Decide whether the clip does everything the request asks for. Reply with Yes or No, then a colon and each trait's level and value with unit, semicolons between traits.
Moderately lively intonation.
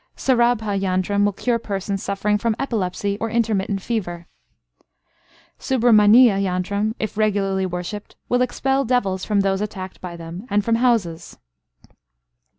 Yes: average, 3.1 semitones